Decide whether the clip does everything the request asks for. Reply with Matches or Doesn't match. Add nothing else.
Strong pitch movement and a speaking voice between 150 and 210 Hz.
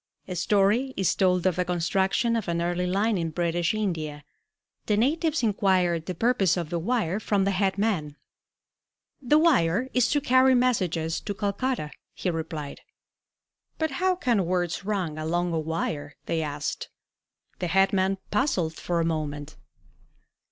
Doesn't match